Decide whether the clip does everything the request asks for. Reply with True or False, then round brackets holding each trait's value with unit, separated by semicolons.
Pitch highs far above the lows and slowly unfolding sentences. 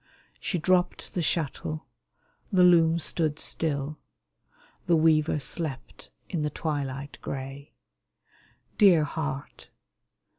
False (2.8 semitones; 100 wpm)